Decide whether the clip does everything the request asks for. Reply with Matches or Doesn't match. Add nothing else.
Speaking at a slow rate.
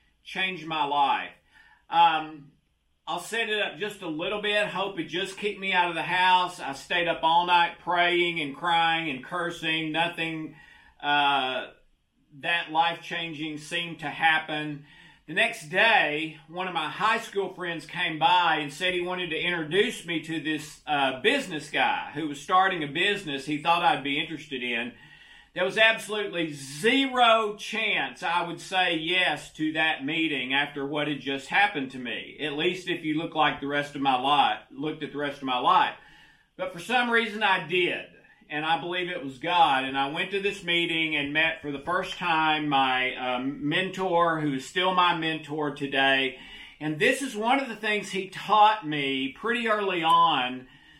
Doesn't match